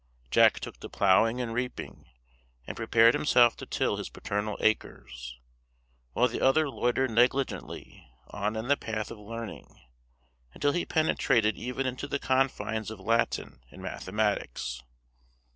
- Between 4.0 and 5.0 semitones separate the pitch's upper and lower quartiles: No, average, 3.5 semitones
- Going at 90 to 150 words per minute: Yes, average, 140 wpm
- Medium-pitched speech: No, low, 115 Hz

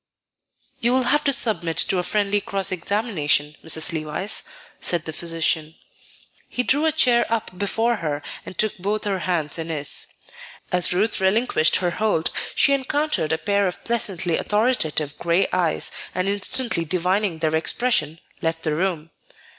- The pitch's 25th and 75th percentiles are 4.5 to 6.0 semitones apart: Yes, average, 5.0 semitones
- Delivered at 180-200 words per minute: No, average, 155 wpm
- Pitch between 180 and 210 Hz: Yes, medium, 185 Hz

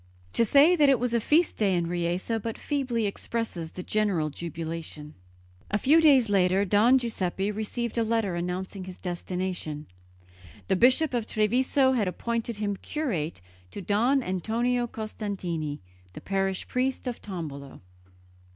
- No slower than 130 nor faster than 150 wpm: Yes, average, 145 wpm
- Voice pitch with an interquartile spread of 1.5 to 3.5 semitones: No, average, 5.1 semitones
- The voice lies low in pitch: No, high, 205 Hz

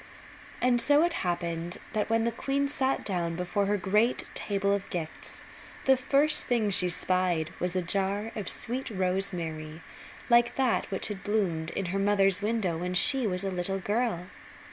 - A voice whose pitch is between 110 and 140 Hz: No, high, 195 Hz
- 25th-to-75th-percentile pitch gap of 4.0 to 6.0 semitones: Yes, average, 4.3 semitones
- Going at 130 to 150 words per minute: No, average, 170 wpm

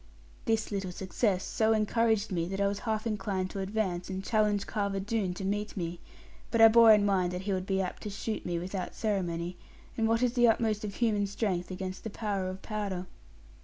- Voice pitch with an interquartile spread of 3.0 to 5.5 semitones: No, narrow, 2.6 semitones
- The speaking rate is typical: No, fast, 210 wpm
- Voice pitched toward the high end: Yes, high, 200 Hz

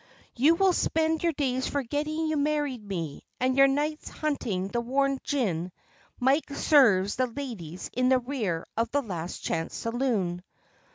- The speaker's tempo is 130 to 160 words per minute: Yes, average, 155 wpm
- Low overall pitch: No, very high, 255 Hz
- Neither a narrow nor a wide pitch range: No, wide, 6.0 semitones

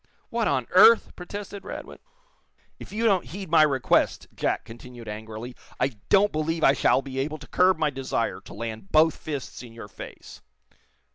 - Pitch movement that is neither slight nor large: No, wide, 7.0 semitones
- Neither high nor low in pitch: Yes, medium, 150 Hz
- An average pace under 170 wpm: No, average, 180 wpm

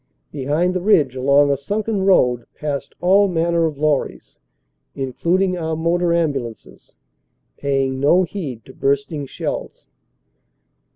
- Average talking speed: No, slow, 120 wpm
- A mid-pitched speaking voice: Yes, medium, 155 Hz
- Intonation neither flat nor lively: Yes, average, 4.4 semitones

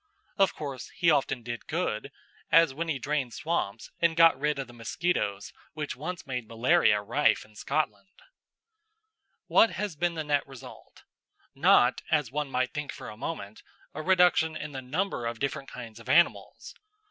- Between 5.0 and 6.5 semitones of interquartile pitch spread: Yes, average, 5.3 semitones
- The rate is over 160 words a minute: Yes, average, 170 wpm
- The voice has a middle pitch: Yes, medium, 145 Hz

